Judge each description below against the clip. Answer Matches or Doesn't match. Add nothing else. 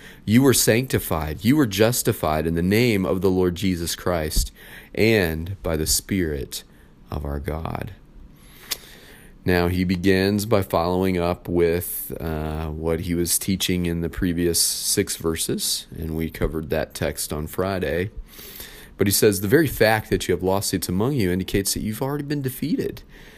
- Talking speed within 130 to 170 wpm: Matches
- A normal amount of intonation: Matches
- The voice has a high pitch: Doesn't match